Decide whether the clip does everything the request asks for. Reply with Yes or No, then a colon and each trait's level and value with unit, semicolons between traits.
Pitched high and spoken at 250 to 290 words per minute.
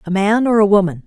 Yes: high, 200 Hz; fast, 280 wpm